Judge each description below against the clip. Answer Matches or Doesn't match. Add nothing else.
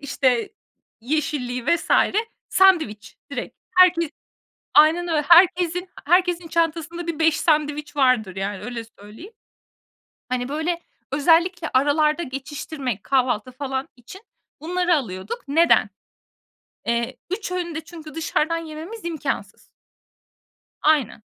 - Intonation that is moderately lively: Matches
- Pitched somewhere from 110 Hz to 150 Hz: Doesn't match